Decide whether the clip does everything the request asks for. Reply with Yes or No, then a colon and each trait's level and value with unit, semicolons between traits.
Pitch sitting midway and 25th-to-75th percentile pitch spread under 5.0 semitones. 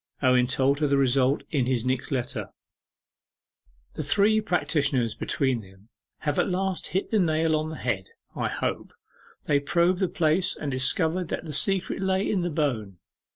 No: medium, 150 Hz; wide, 5.6 semitones